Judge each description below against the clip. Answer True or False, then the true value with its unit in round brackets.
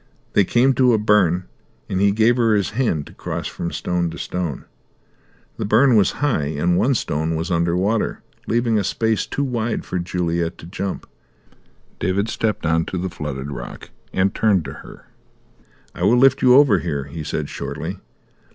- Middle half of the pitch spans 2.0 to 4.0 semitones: False (5.1 semitones)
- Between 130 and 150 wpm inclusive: False (180 wpm)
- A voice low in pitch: True (95 Hz)